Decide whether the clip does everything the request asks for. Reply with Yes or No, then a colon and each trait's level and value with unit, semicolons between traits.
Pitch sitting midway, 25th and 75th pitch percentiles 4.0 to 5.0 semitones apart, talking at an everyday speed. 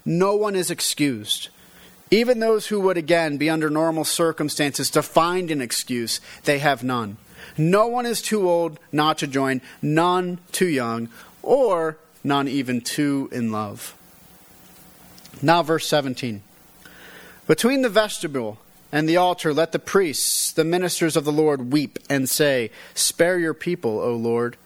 Yes: medium, 155 Hz; average, 4.5 semitones; average, 150 wpm